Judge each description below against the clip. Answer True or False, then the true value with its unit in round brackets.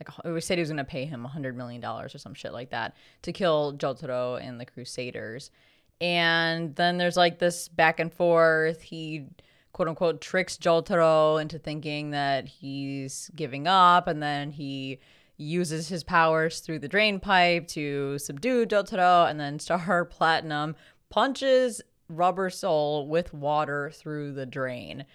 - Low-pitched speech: False (160 Hz)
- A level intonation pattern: False (3.4 semitones)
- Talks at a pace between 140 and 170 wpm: True (155 wpm)